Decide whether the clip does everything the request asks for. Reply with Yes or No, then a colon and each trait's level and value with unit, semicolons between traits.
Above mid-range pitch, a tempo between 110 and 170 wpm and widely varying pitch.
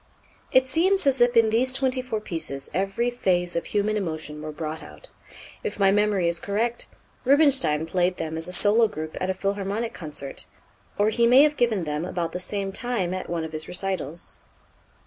No: high, 195 Hz; average, 190 wpm; wide, 6.0 semitones